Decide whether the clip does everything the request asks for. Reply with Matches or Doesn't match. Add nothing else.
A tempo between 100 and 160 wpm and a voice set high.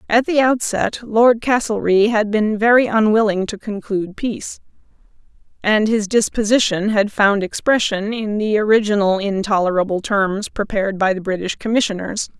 Matches